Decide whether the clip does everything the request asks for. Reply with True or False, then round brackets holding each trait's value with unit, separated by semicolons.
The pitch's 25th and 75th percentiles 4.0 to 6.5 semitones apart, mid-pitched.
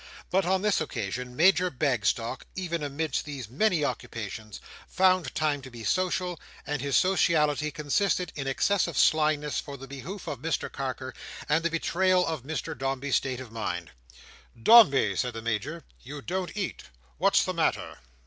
True (5.4 semitones; 150 Hz)